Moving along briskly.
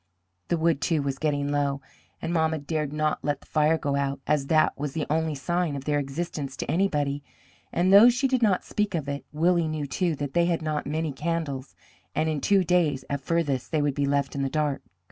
Yes: fast, 220 wpm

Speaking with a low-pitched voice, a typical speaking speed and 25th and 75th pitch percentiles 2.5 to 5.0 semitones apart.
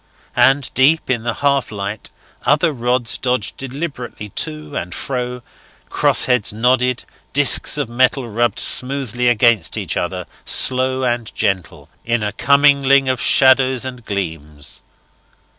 No: low, 125 Hz; slow, 125 wpm; average, 3.6 semitones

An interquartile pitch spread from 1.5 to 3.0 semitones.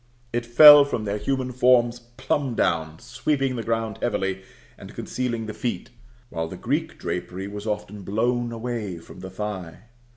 No: average, 3.7 semitones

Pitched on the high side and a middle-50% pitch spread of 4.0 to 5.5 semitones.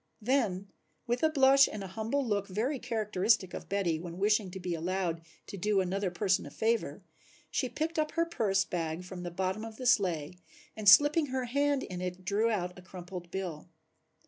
Yes: high, 200 Hz; average, 4.7 semitones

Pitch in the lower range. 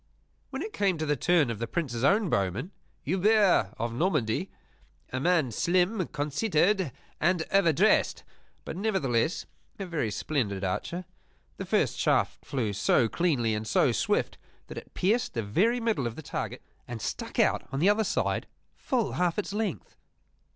No: medium, 165 Hz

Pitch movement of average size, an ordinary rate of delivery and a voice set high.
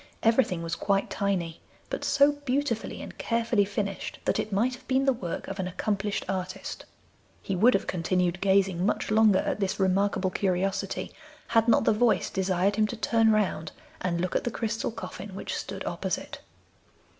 Yes: average, 3.3 semitones; average, 175 wpm; high, 200 Hz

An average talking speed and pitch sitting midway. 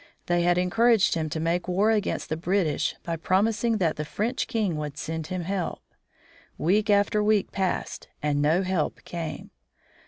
Yes: average, 165 wpm; medium, 180 Hz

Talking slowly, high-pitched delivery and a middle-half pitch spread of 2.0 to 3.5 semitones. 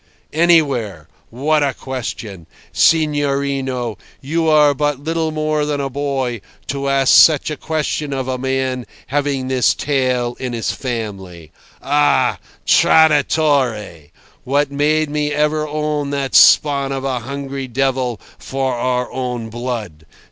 No: slow, 130 wpm; low, 135 Hz; average, 2.9 semitones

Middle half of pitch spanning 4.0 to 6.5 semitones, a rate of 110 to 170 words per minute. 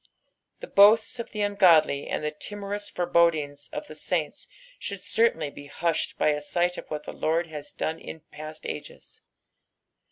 Yes: average, 4.7 semitones; average, 165 wpm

